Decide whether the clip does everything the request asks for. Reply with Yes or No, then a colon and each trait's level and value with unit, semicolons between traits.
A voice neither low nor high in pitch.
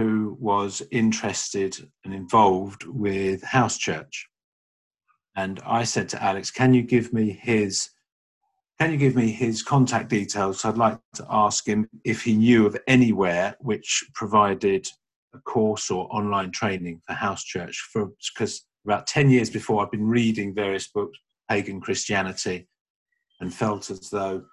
No: low, 110 Hz